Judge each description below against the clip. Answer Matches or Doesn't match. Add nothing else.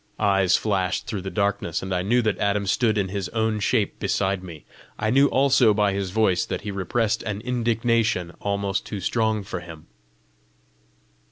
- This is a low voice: Matches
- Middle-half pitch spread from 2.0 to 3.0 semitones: Matches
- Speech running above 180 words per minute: Doesn't match